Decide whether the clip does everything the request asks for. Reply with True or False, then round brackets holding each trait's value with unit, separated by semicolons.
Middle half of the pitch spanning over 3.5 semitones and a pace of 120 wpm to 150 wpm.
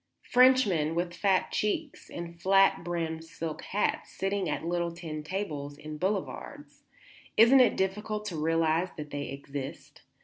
True (4.0 semitones; 140 wpm)